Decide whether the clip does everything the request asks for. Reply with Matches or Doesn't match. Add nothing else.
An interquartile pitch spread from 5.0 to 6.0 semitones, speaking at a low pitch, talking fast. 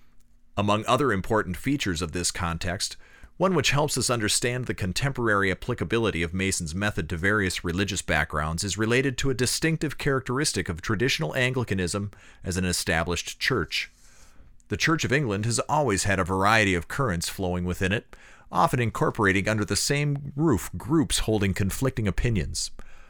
Doesn't match